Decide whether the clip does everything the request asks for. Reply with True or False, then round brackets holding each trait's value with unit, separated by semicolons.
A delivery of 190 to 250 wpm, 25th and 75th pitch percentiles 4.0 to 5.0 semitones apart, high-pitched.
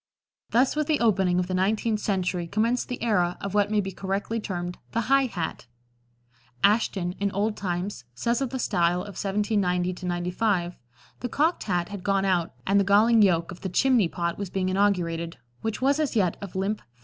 False (195 wpm; 3.6 semitones; 195 Hz)